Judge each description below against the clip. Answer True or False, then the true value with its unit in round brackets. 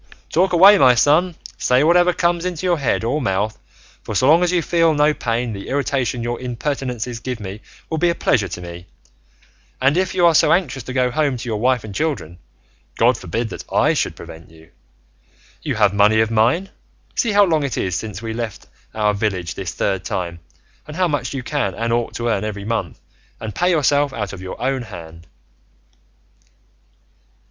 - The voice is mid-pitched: False (125 Hz)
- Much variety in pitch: True (6.5 semitones)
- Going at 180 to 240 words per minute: True (195 wpm)